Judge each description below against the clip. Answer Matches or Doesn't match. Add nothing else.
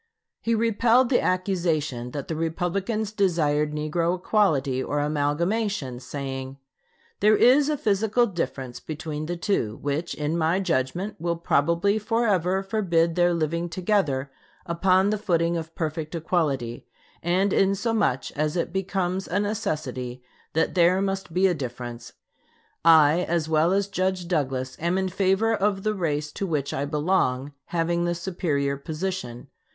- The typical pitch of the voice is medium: Matches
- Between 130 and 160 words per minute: Matches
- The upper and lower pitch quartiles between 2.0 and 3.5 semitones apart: Doesn't match